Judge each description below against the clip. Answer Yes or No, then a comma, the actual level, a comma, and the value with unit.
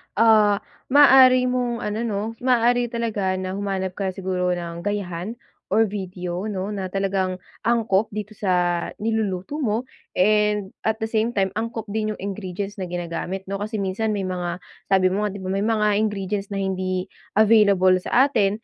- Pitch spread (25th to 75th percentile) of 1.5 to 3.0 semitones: Yes, average, 2.7 semitones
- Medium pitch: No, high, 200 Hz